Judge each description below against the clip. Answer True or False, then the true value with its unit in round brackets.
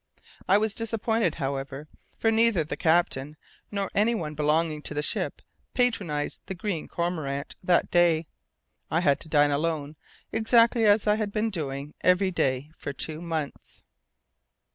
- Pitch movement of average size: False (5.7 semitones)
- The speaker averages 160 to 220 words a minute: False (145 wpm)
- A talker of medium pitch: True (165 Hz)